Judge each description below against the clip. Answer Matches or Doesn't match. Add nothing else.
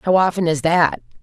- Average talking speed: Matches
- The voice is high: Doesn't match